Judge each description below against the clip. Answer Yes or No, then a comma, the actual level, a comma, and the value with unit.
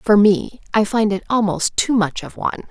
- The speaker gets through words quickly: Yes, fast, 220 wpm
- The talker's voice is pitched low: No, high, 205 Hz